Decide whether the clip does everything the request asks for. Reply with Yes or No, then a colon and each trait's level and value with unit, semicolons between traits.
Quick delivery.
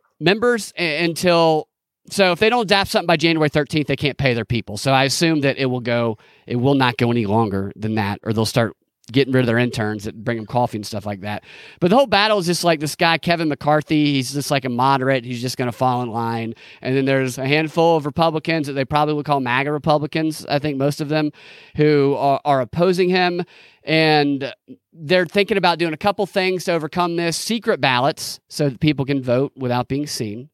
Yes: fast, 225 wpm